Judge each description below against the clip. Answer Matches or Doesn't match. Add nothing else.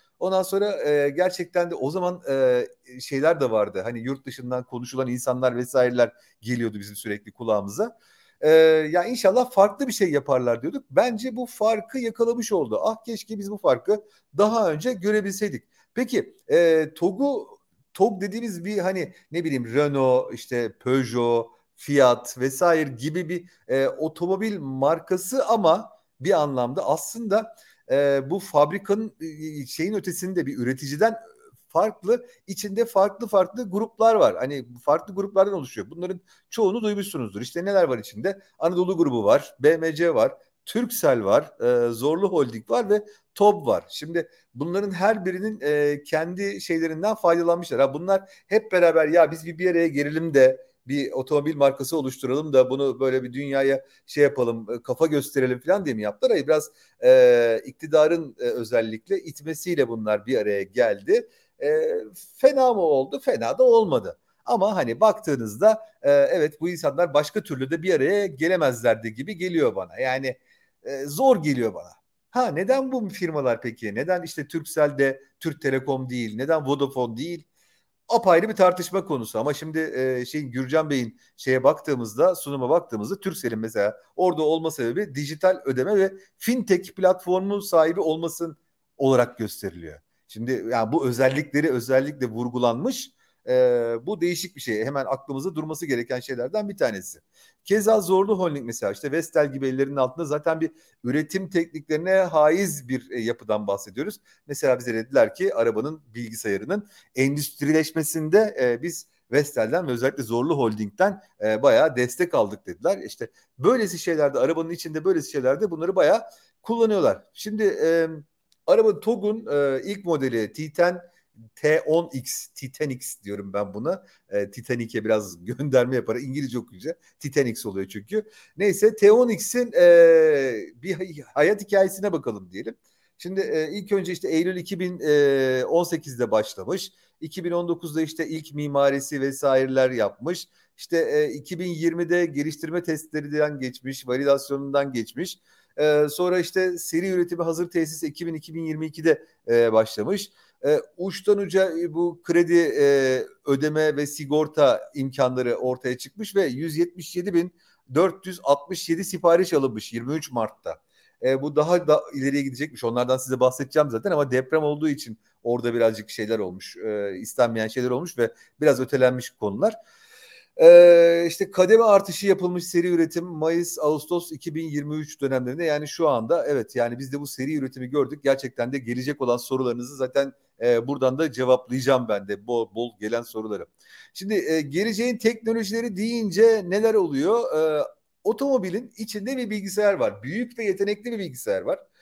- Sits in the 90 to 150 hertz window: Doesn't match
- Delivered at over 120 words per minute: Matches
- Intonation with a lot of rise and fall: Matches